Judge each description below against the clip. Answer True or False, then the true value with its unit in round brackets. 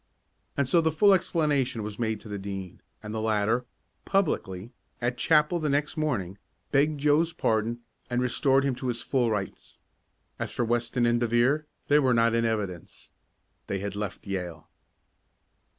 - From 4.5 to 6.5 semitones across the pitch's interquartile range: True (5.2 semitones)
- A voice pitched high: False (120 Hz)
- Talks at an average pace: True (165 wpm)